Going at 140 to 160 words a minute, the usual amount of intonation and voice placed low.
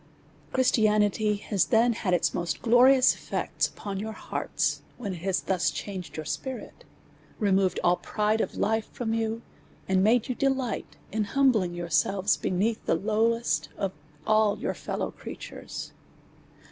No: average, 145 wpm; average, 3.3 semitones; high, 215 Hz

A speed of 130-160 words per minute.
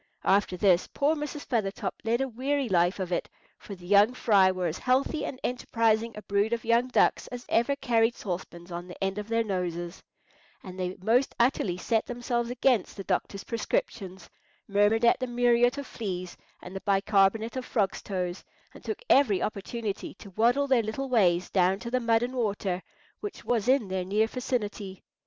No: average, 185 wpm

